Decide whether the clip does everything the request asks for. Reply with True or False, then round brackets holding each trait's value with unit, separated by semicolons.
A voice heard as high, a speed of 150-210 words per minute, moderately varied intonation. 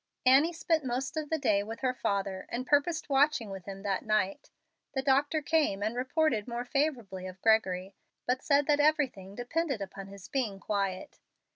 False (245 Hz; 175 wpm; 6.5 semitones)